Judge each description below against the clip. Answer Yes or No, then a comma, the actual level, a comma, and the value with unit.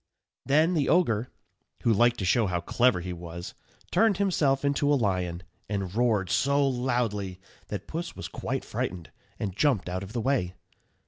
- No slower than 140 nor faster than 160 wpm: No, average, 170 wpm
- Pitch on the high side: No, low, 115 Hz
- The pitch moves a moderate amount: No, wide, 7.0 semitones